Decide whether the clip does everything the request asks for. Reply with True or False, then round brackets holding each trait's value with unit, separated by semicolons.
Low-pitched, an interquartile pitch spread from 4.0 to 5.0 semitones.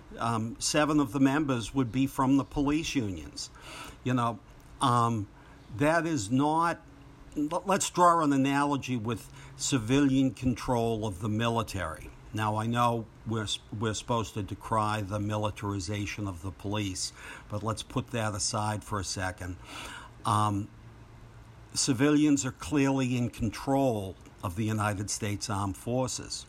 True (115 Hz; 4.6 semitones)